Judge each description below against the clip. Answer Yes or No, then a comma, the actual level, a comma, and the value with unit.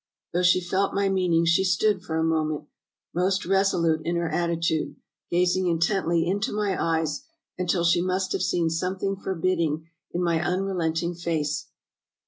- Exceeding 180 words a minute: No, average, 160 wpm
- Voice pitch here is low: No, medium, 175 Hz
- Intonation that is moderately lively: No, narrow, 2.2 semitones